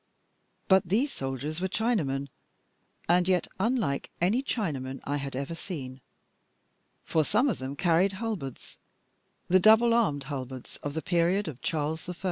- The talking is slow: No, average, 145 wpm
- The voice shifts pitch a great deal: Yes, wide, 6.3 semitones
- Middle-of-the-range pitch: Yes, medium, 170 Hz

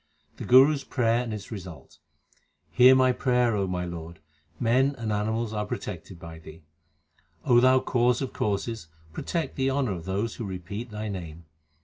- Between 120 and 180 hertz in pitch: No, low, 110 Hz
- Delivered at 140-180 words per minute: Yes, average, 170 wpm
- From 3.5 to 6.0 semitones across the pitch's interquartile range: Yes, average, 5.2 semitones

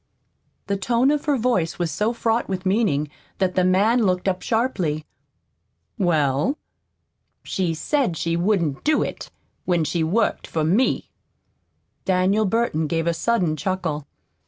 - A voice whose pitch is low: No, medium, 185 Hz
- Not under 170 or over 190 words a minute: No, average, 140 wpm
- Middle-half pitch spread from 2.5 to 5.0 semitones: No, wide, 5.6 semitones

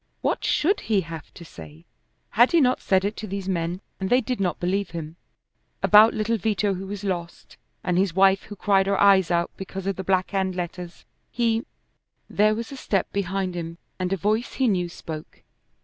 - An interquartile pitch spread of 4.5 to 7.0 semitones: No, average, 2.9 semitones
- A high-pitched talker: Yes, high, 195 Hz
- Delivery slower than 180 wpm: No, average, 200 wpm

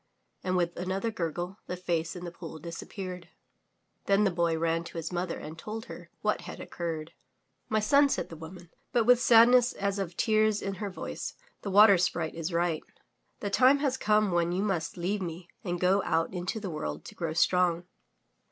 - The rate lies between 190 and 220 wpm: Yes, average, 195 wpm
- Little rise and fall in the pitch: No, average, 3.5 semitones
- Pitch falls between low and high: Yes, medium, 180 Hz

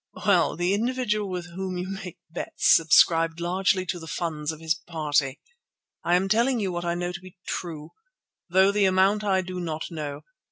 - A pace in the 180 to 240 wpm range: Yes, average, 190 wpm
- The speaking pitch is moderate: Yes, medium, 180 Hz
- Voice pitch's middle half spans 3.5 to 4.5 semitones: No, narrow, 2.6 semitones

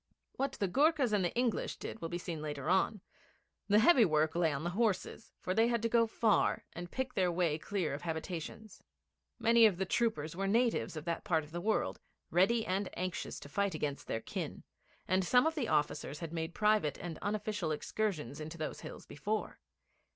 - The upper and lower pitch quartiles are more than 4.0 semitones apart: Yes, wide, 5.4 semitones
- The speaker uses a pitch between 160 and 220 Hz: Yes, medium, 185 Hz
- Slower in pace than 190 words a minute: No, average, 200 wpm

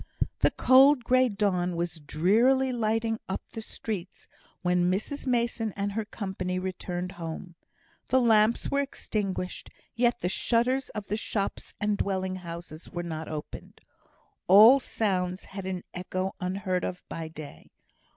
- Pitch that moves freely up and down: No, average, 4.0 semitones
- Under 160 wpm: Yes, average, 140 wpm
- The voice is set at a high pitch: Yes, high, 195 Hz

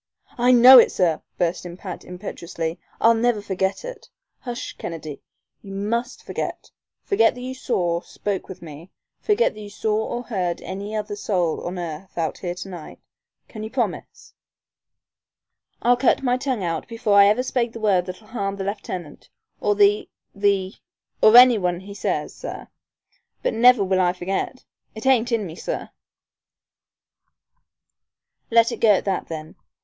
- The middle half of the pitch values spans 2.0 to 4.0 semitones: No, average, 4.6 semitones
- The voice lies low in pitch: No, high, 205 Hz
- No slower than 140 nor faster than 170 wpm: Yes, average, 165 wpm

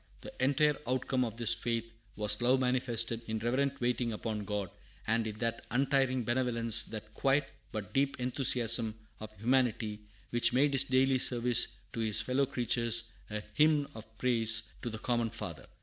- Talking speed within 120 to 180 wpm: Yes, average, 165 wpm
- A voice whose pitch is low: Yes, low, 120 Hz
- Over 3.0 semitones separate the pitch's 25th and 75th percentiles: No, average, 2.7 semitones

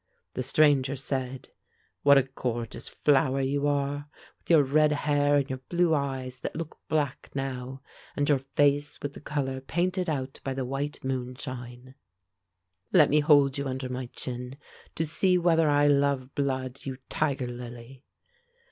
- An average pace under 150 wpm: No, average, 155 wpm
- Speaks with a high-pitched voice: No, low, 135 Hz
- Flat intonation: Yes, narrow, 2.0 semitones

